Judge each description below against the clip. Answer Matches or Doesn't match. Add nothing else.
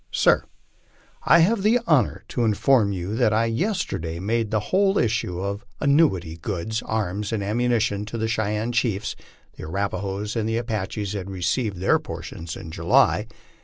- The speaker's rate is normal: Matches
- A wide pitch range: Doesn't match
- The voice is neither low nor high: Doesn't match